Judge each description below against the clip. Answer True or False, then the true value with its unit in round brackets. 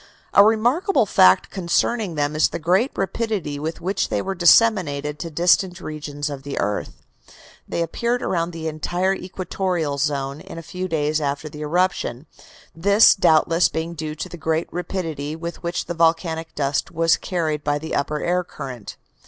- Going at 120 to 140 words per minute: False (170 wpm)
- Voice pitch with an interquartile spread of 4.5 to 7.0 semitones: False (3.4 semitones)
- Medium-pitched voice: True (165 Hz)